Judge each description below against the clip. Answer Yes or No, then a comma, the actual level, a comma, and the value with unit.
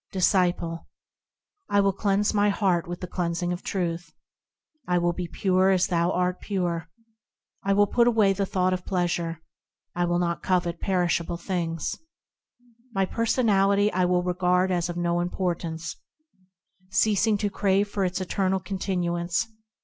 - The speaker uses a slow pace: No, average, 150 wpm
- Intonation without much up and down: Yes, narrow, 2.1 semitones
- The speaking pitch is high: No, medium, 180 Hz